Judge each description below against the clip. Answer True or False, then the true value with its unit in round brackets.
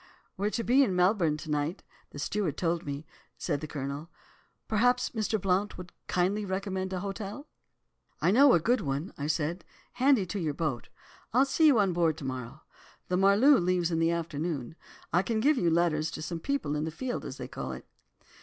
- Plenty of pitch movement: False (5.0 semitones)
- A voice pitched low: False (180 Hz)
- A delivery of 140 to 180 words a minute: False (200 wpm)